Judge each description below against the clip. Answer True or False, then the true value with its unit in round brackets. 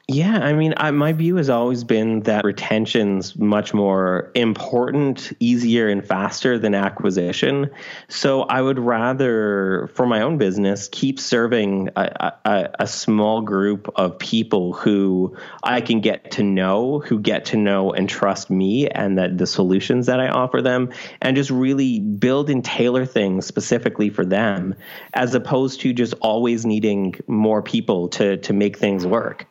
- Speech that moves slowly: False (165 wpm)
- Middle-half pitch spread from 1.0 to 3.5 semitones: False (4.5 semitones)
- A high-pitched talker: False (110 Hz)